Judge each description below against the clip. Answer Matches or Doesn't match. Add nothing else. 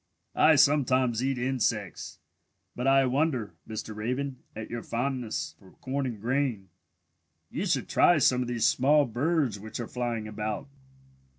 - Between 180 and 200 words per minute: Doesn't match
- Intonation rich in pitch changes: Doesn't match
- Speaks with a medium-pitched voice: Doesn't match